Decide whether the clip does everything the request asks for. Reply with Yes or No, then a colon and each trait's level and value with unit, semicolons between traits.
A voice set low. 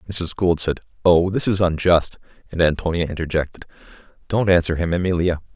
Yes: very low, 85 Hz